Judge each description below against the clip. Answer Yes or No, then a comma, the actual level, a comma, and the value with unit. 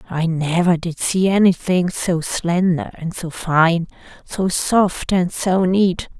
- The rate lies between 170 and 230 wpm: No, average, 145 wpm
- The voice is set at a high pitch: No, medium, 175 Hz